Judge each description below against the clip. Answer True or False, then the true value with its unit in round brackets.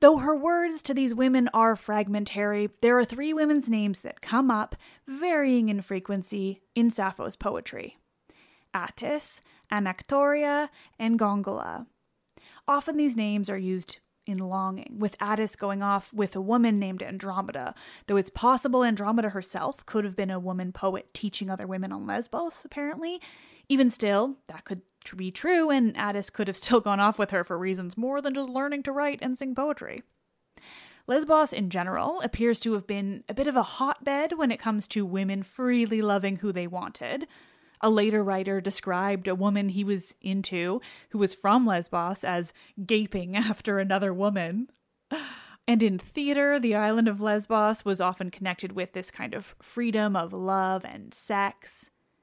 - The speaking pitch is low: False (210 Hz)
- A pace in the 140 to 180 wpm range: True (165 wpm)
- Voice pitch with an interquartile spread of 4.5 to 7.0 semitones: True (4.9 semitones)